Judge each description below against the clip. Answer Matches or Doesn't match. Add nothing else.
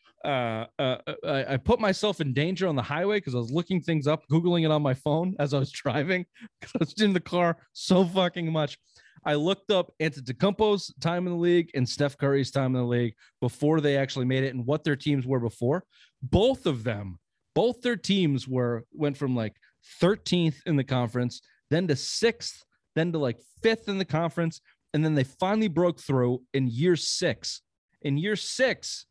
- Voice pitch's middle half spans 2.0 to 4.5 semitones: Doesn't match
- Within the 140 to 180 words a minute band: Doesn't match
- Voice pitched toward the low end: Doesn't match